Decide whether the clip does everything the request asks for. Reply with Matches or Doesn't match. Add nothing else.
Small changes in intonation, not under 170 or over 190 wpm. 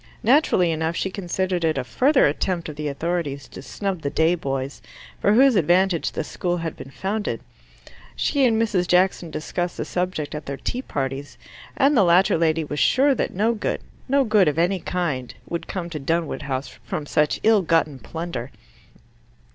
Doesn't match